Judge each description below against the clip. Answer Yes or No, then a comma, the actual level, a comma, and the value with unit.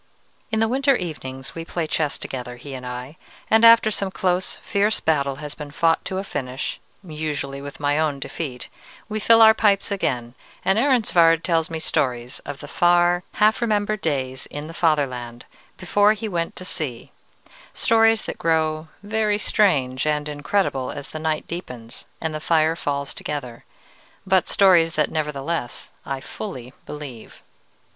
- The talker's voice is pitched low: No, medium, 160 Hz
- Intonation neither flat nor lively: No, wide, 5.7 semitones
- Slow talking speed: No, average, 160 wpm